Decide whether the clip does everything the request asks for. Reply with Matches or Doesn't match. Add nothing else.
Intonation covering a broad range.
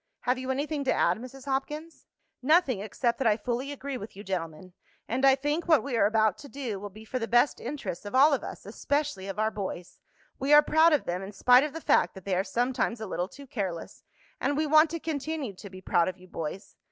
Matches